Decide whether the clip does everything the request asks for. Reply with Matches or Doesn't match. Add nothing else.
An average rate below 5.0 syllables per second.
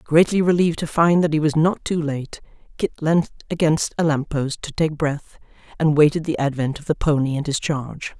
Doesn't match